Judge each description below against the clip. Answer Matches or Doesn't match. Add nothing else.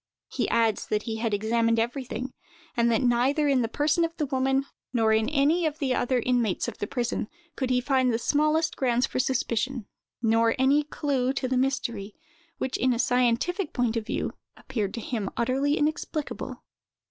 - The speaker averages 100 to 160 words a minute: Doesn't match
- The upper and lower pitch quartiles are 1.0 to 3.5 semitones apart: Matches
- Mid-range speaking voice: Doesn't match